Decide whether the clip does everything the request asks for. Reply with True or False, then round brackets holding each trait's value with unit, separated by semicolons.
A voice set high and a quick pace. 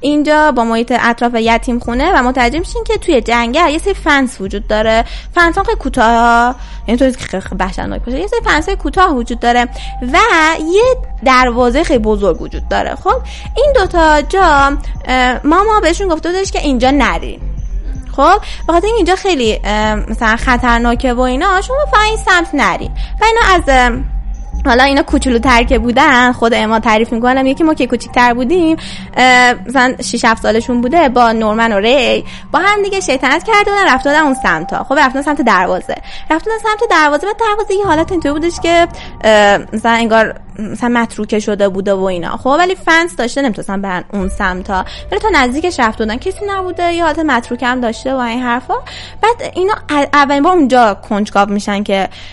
True (260 Hz; 170 wpm)